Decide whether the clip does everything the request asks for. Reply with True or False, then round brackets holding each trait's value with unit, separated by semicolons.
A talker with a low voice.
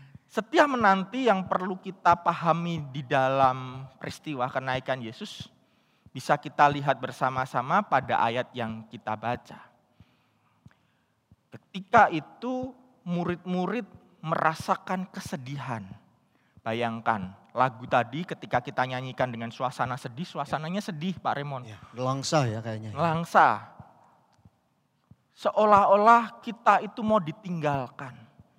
False (150 Hz)